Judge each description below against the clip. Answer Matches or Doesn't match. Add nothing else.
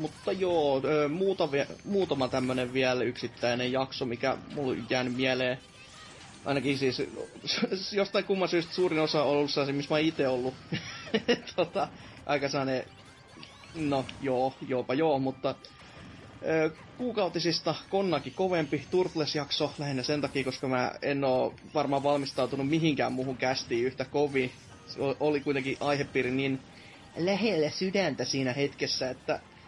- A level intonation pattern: Doesn't match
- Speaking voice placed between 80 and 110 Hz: Doesn't match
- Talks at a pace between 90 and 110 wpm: Doesn't match